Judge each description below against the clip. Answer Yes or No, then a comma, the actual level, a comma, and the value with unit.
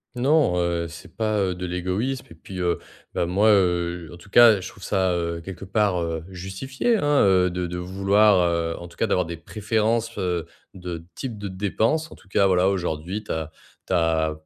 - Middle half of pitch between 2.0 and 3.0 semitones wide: No, average, 3.4 semitones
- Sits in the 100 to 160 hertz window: No, very low, 90 Hz